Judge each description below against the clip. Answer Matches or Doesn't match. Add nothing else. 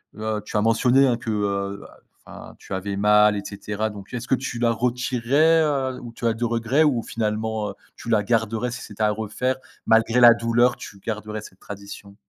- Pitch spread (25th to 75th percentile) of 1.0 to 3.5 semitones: Matches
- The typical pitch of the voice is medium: Doesn't match